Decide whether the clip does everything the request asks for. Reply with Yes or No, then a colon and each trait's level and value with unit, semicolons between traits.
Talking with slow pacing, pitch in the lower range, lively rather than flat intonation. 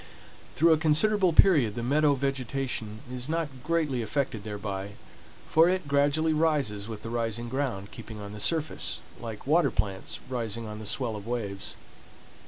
No: average, 160 wpm; low, 125 Hz; wide, 5.9 semitones